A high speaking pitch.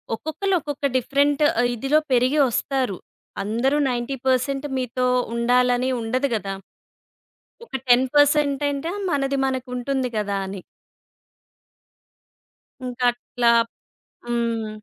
Yes: very high, 255 Hz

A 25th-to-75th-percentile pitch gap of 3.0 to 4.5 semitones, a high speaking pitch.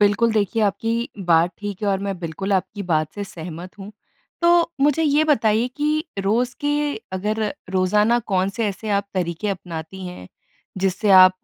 Yes: average, 3.5 semitones; high, 200 Hz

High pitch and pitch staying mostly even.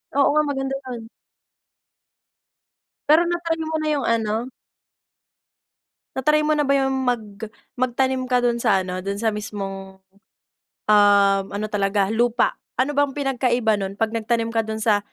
No: high, 235 Hz; average, 4.4 semitones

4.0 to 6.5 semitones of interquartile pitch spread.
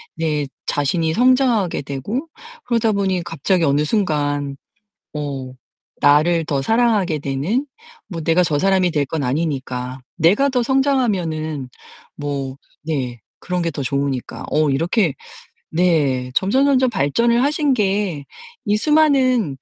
No: wide, 7.4 semitones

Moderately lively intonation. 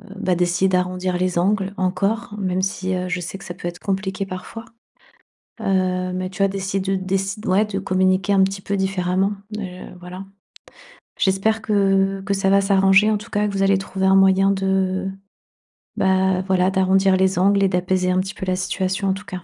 No: narrow, 1.0 semitones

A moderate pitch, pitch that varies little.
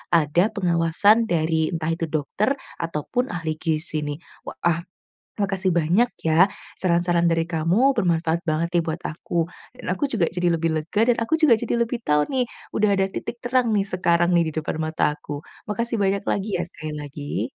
No: medium, 170 Hz; average, 3.9 semitones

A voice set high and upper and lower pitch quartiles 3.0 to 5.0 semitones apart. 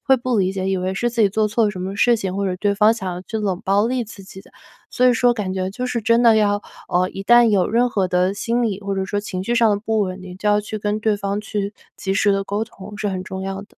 No: high, 205 Hz; narrow, 2.5 semitones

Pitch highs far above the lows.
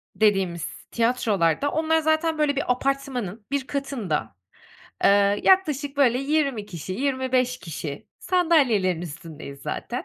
Yes: wide, 7.0 semitones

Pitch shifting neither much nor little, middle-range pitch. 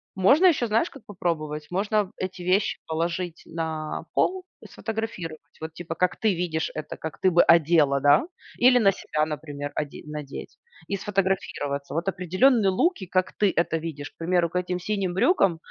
Yes: average, 3.8 semitones; medium, 175 Hz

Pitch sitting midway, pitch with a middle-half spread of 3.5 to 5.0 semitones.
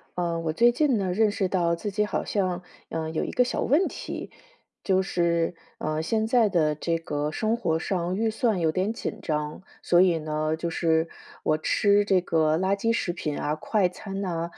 Yes: medium, 180 Hz; average, 4.2 semitones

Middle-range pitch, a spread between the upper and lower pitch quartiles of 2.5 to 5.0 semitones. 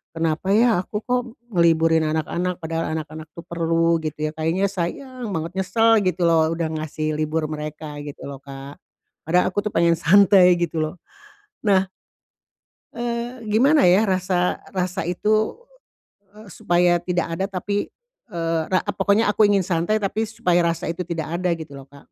Yes: medium, 175 Hz; average, 3.8 semitones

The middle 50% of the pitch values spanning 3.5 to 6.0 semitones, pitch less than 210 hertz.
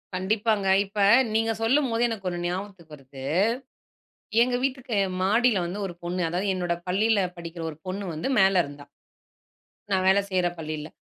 Yes: average, 4.0 semitones; high, 190 Hz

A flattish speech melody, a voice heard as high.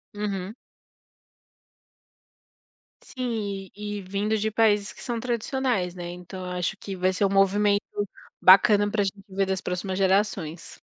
Yes: narrow, 1.9 semitones; high, 200 Hz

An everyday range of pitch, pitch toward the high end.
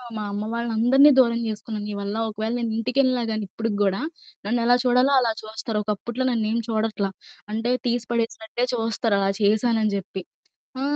No: narrow, 2.0 semitones; high, 225 Hz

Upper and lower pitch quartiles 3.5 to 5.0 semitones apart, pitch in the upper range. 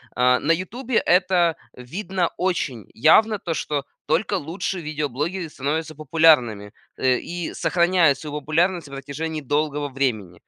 No: average, 4.1 semitones; medium, 155 Hz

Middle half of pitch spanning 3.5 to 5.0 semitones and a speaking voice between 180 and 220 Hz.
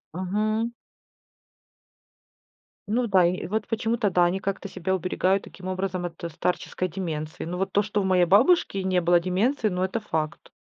No: narrow, 2.6 semitones; high, 190 Hz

